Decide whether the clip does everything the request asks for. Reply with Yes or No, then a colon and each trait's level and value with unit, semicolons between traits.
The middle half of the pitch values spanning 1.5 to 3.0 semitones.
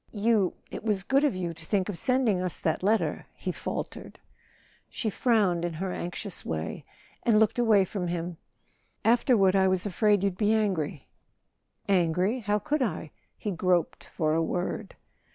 No: average, 3.8 semitones